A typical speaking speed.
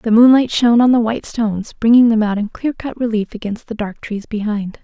No: fast, 235 wpm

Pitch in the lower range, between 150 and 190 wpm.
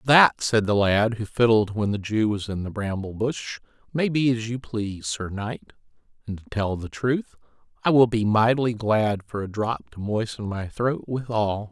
No: low, 110 Hz; average, 200 wpm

